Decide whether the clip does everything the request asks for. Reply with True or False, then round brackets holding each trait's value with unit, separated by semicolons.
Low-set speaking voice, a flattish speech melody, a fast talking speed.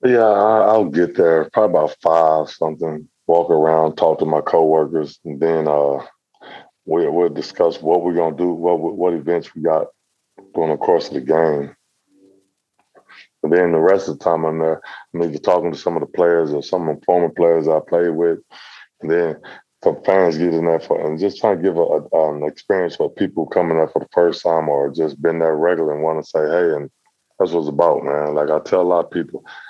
True (80 Hz; 1.7 semitones; 220 wpm)